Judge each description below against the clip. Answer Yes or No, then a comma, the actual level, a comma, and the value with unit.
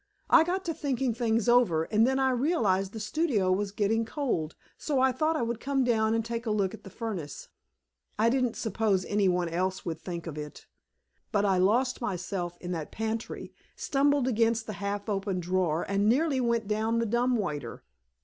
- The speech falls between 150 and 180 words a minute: No, average, 195 wpm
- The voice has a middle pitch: No, high, 220 Hz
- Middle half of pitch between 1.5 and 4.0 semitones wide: No, average, 4.6 semitones